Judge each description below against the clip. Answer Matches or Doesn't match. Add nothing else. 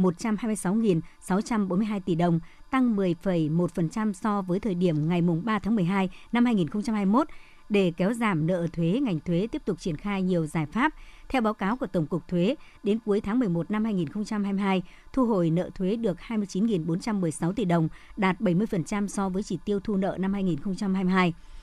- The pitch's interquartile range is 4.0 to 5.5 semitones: Doesn't match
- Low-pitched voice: Doesn't match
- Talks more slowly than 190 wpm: Matches